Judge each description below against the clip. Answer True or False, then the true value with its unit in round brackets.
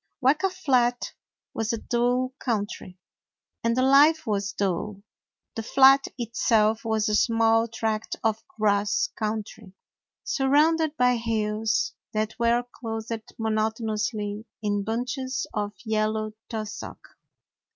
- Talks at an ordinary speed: False (115 wpm)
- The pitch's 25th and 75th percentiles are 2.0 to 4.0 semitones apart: True (2.6 semitones)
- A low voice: False (225 Hz)